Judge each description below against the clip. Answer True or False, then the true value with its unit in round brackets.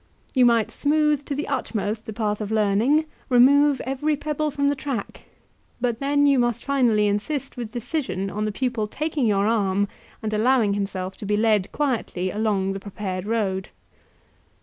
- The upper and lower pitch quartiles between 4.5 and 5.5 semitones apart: True (5.2 semitones)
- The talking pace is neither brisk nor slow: True (170 wpm)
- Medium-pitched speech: False (230 Hz)